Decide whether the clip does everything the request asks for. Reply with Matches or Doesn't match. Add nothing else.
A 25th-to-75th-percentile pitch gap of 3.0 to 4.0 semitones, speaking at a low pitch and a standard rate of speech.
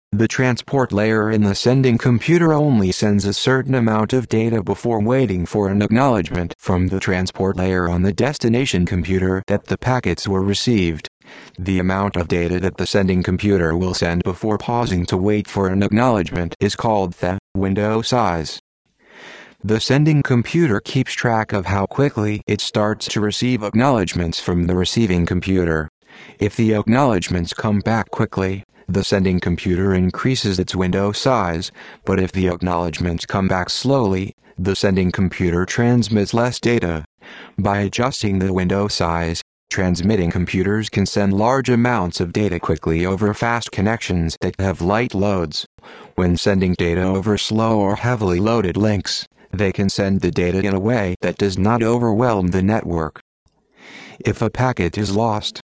Matches